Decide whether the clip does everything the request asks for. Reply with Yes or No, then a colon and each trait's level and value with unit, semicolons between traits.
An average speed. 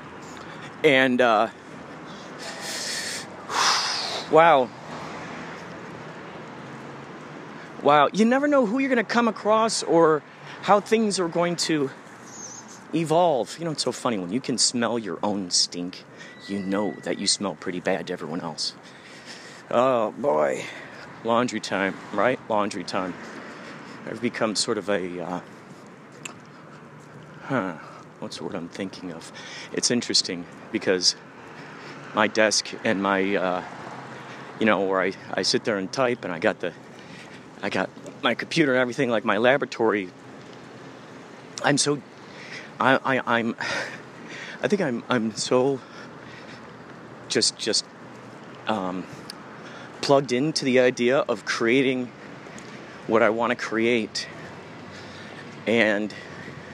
No: slow, 125 wpm